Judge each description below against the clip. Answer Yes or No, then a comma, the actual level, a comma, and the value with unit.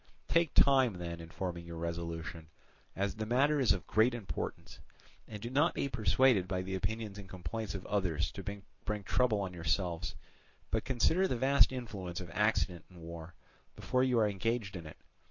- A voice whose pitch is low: Yes, low, 100 Hz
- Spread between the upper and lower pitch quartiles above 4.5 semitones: Yes, wide, 5.5 semitones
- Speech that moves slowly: No, average, 180 wpm